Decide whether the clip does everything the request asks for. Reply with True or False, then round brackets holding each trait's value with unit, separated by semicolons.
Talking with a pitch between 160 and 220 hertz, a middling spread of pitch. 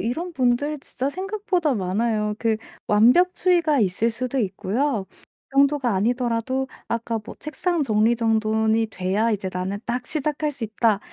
False (235 Hz; 5.0 semitones)